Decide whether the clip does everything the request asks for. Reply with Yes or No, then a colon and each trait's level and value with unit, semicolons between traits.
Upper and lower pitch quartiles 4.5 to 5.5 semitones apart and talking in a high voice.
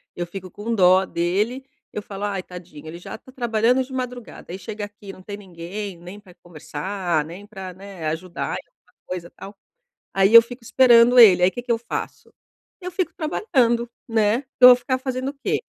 Yes: average, 4.9 semitones; high, 205 Hz